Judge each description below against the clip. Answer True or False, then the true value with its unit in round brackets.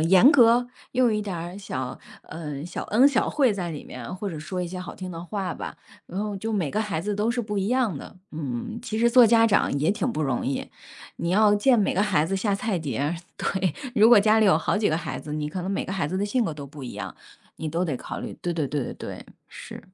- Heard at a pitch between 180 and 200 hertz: True (190 Hz)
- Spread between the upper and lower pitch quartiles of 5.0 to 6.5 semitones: True (5.5 semitones)